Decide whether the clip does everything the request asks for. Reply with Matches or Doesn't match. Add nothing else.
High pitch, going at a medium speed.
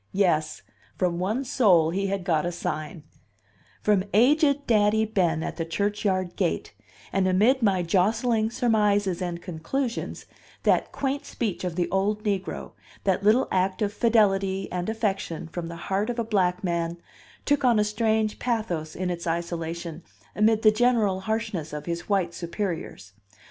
Matches